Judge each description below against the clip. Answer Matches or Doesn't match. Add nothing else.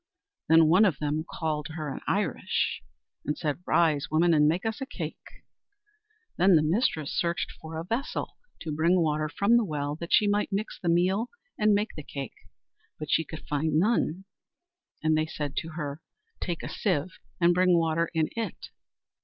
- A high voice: Doesn't match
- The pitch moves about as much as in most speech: Matches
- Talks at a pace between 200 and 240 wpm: Doesn't match